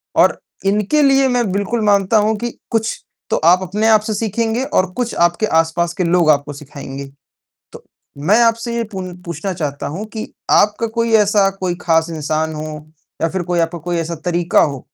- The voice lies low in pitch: No, high, 190 Hz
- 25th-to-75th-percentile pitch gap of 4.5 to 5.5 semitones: Yes, average, 5.0 semitones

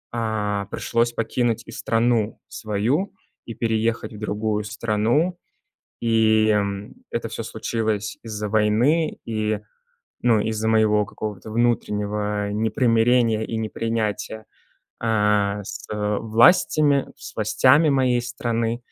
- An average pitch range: No, narrow, 1.9 semitones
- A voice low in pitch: Yes, low, 110 Hz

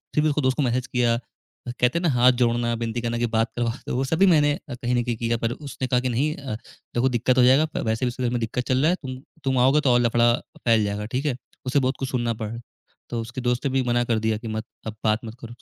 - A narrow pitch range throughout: Yes, narrow, 1.9 semitones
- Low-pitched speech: Yes, low, 120 Hz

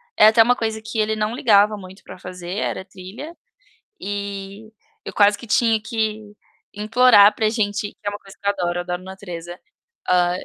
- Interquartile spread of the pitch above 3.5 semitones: No, narrow, 2.6 semitones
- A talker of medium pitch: No, high, 205 Hz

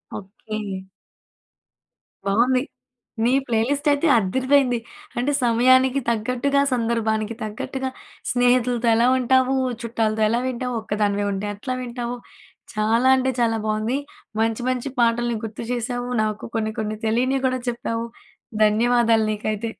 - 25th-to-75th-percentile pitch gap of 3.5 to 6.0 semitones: No, average, 2.7 semitones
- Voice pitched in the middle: No, high, 235 Hz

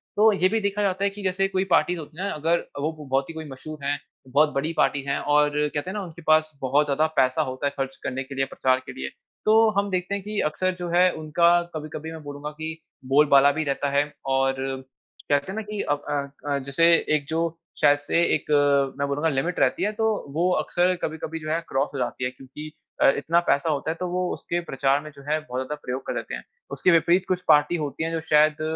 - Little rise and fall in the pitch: No, average, 3.7 semitones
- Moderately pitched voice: Yes, medium, 155 Hz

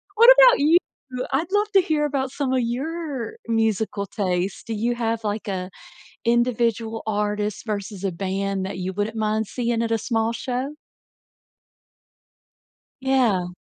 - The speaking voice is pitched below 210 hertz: No, high, 225 Hz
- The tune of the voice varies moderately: Yes, average, 4.1 semitones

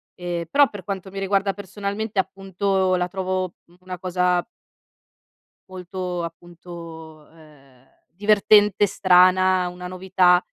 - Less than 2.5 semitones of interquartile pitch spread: Yes, narrow, 1.7 semitones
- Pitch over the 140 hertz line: Yes, medium, 185 Hz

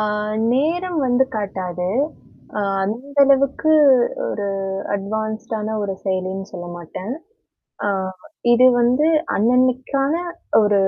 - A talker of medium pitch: No, high, 220 Hz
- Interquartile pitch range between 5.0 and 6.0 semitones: Yes, average, 5.3 semitones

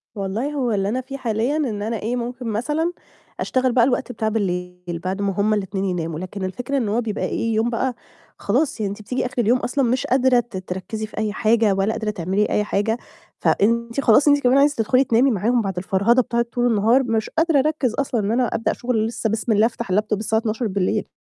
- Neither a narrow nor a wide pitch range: Yes, average, 3.4 semitones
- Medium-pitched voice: No, high, 225 Hz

